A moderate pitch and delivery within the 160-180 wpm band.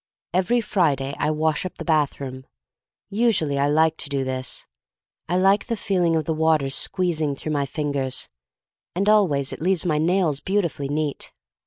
Yes: medium, 155 Hz; average, 170 wpm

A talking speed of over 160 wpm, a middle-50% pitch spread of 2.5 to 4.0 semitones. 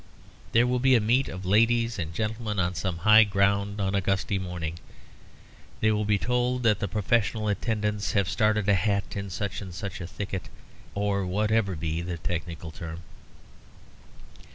Yes: average, 170 wpm; average, 2.9 semitones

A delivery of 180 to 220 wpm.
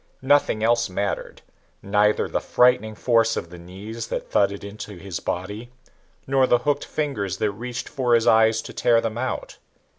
No: average, 170 wpm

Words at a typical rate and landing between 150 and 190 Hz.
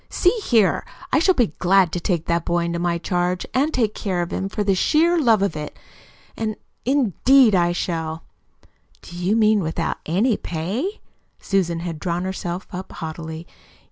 Yes: average, 170 wpm; medium, 185 Hz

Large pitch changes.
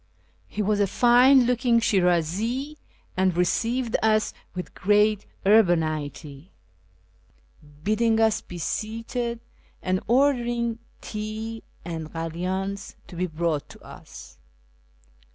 No: average, 4.7 semitones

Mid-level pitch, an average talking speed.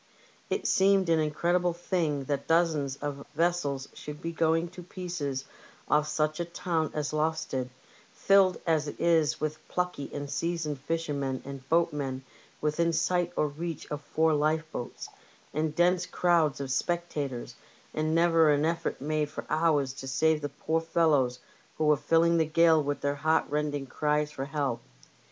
Yes: medium, 155 Hz; average, 160 wpm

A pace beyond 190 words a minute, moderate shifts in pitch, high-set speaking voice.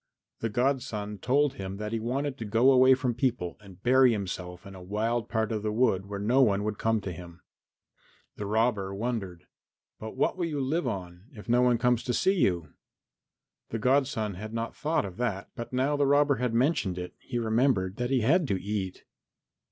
No: average, 200 wpm; average, 4.4 semitones; low, 115 Hz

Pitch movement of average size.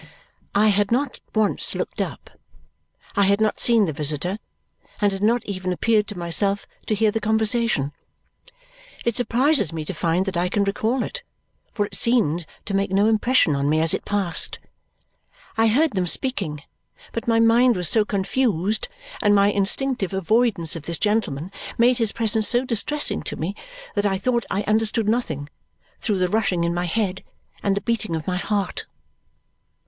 Yes: average, 3.9 semitones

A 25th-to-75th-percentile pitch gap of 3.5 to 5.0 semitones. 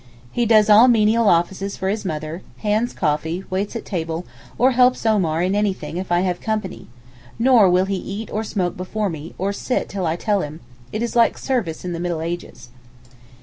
Yes: average, 4.2 semitones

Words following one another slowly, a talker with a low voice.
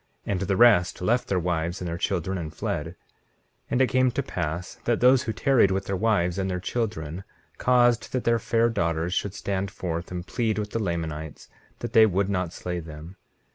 No: fast, 205 wpm; very low, 95 Hz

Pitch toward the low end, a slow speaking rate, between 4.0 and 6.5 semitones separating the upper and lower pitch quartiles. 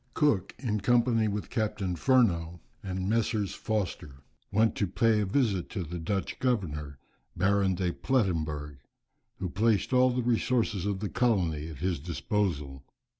No: low, 100 Hz; average, 145 wpm; average, 4.9 semitones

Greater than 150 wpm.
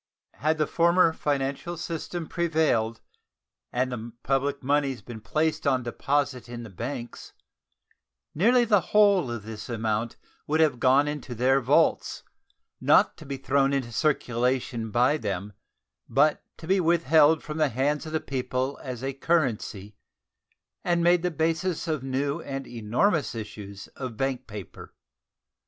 No: average, 145 wpm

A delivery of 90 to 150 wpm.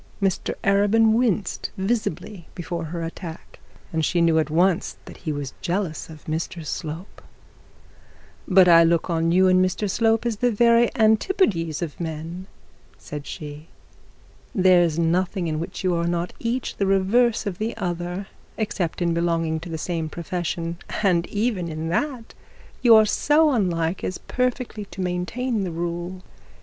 No: average, 160 wpm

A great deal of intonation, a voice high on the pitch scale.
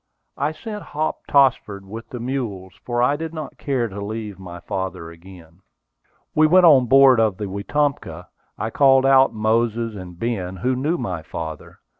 No: wide, 6.1 semitones; low, 115 Hz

